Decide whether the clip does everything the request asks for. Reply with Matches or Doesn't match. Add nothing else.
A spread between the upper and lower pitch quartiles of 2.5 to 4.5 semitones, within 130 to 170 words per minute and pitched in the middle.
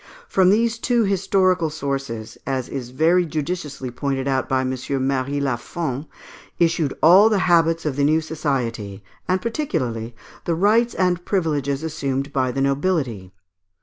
Doesn't match